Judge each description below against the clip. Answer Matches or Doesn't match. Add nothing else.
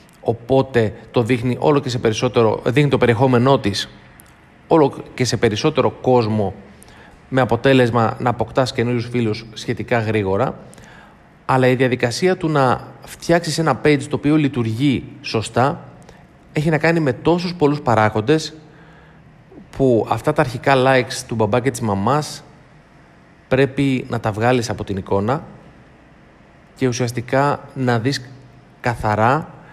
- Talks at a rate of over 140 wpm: Doesn't match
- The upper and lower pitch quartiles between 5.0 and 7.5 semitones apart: Doesn't match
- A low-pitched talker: Matches